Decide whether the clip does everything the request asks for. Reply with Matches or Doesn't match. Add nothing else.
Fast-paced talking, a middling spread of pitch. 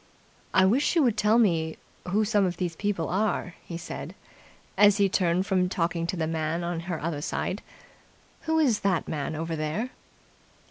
Doesn't match